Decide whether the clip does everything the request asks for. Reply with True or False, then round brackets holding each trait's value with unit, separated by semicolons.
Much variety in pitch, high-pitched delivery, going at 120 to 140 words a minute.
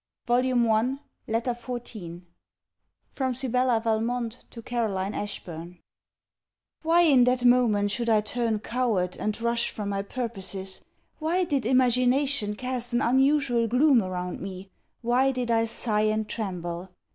False (3.3 semitones; 235 Hz; 135 wpm)